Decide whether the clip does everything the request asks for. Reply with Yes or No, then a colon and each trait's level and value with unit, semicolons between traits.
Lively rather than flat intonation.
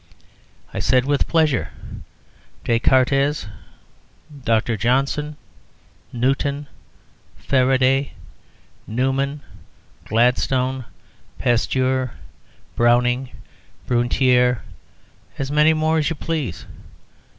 No: narrow, 2.4 semitones